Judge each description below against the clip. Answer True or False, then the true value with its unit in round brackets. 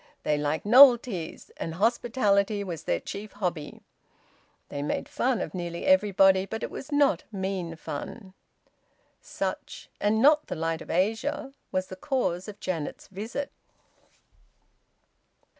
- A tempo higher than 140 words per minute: False (135 wpm)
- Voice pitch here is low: False (200 Hz)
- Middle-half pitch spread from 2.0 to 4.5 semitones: False (5.4 semitones)